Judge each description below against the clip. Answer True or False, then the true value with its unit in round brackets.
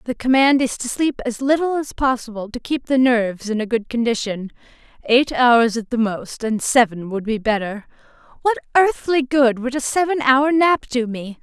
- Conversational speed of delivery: True (190 wpm)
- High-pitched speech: True (250 Hz)